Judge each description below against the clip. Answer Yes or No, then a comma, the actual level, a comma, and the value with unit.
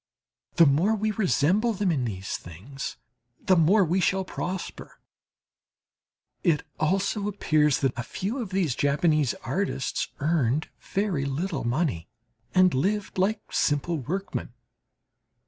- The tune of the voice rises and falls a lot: Yes, wide, 5.8 semitones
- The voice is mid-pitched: Yes, medium, 170 Hz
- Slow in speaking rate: Yes, slow, 125 wpm